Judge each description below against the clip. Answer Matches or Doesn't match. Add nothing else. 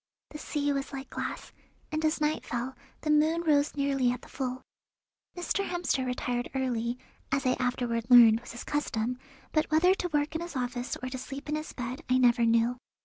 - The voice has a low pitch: Doesn't match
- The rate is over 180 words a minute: Matches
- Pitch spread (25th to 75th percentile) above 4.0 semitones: Doesn't match